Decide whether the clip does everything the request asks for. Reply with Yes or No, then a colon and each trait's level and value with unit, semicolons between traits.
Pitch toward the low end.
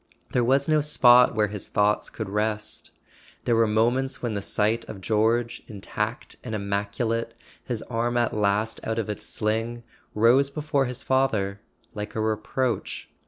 Yes: low, 110 Hz